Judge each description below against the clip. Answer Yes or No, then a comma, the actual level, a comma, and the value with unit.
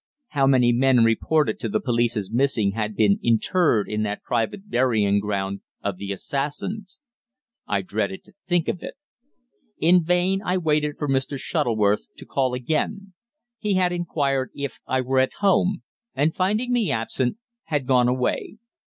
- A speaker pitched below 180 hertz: Yes, low, 135 Hz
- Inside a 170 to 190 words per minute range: No, average, 160 wpm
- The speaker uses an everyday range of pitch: No, wide, 7.8 semitones